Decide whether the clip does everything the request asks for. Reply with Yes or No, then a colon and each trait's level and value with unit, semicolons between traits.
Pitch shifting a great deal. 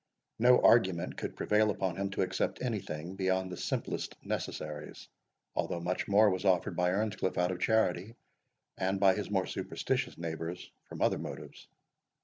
No: narrow, 2.6 semitones